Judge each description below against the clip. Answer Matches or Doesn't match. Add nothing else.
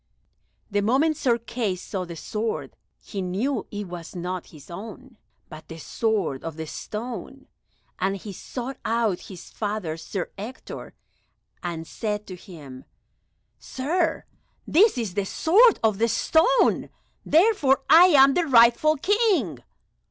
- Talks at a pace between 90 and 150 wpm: Matches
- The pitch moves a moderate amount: Doesn't match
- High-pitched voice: Matches